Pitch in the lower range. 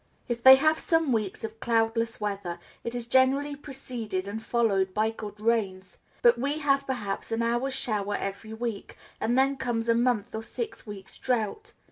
No: high, 230 Hz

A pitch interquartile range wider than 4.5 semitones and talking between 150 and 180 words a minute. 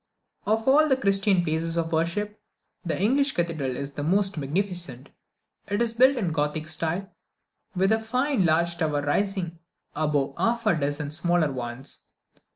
Yes: average, 5.1 semitones; average, 160 wpm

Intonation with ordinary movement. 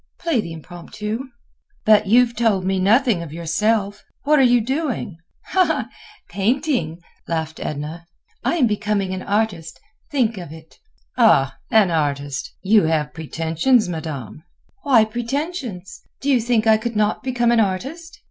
No: wide, 6.3 semitones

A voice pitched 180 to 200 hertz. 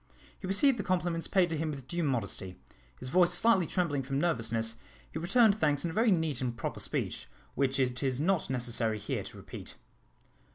No: medium, 155 Hz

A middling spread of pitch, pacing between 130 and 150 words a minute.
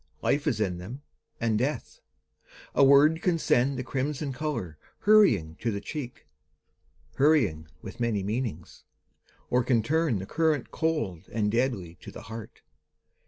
No: wide, 6.2 semitones; average, 145 wpm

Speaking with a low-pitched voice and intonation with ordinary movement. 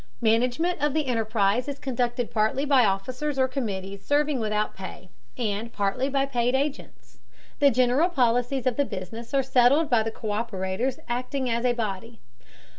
No: high, 245 Hz; average, 3.7 semitones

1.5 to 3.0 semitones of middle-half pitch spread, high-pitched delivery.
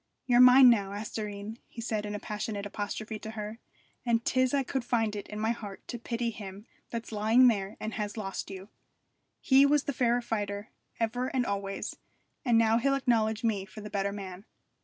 Yes: average, 2.7 semitones; high, 220 Hz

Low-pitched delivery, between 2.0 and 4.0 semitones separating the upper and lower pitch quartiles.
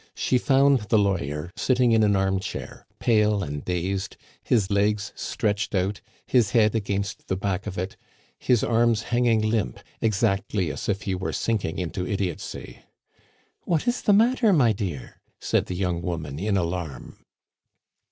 Yes: low, 100 Hz; average, 3.6 semitones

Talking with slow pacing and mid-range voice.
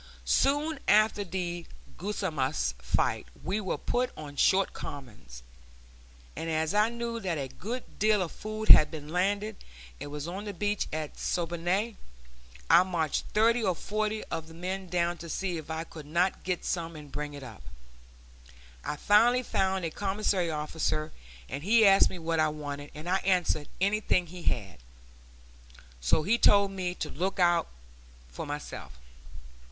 No: average, 160 wpm; medium, 175 Hz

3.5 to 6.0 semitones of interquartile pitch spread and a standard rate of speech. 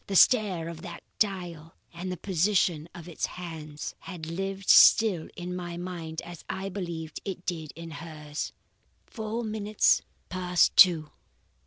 No: average, 2.9 semitones; average, 145 wpm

